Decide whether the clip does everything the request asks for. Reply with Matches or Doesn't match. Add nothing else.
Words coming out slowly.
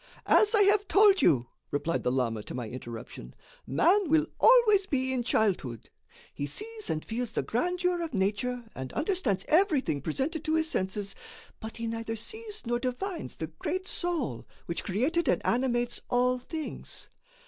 Doesn't match